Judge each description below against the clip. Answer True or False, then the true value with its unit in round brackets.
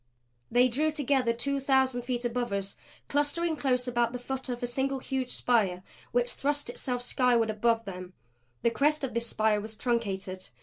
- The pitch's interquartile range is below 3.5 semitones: True (2.7 semitones)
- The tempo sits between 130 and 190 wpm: True (175 wpm)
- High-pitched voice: True (245 Hz)